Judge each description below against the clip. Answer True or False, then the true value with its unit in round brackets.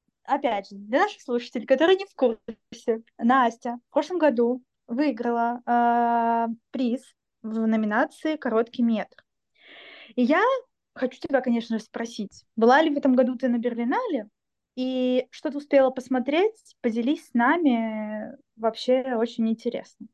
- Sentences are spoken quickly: False (135 wpm)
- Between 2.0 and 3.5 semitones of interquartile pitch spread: True (3.0 semitones)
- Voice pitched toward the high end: True (245 Hz)